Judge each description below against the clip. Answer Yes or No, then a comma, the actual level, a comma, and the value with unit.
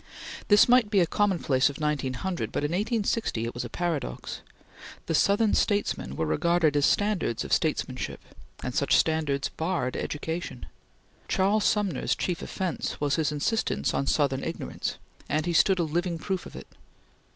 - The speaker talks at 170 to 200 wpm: No, average, 155 wpm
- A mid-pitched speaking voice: Yes, medium, 165 Hz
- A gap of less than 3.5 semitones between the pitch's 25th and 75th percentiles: No, average, 5.1 semitones